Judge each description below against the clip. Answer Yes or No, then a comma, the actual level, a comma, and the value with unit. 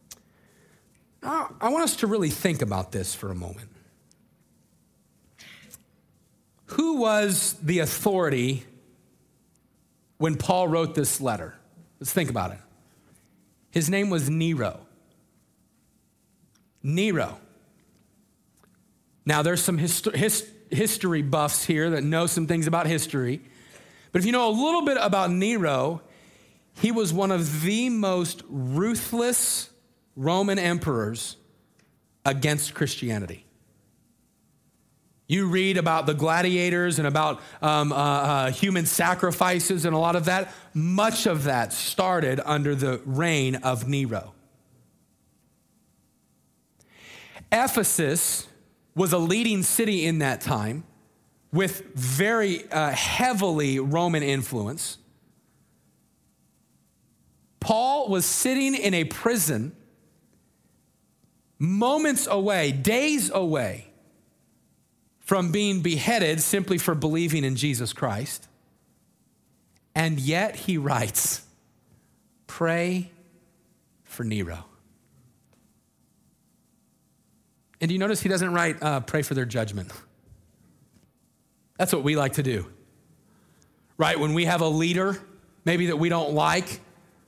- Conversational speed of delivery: No, slow, 110 wpm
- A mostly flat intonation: No, wide, 5.4 semitones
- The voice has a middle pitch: Yes, medium, 165 Hz